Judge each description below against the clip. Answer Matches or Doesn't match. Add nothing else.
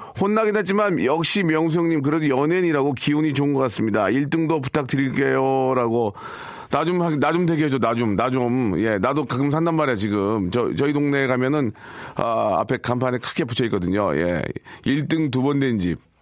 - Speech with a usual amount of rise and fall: Matches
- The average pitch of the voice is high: Doesn't match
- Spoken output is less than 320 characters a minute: Doesn't match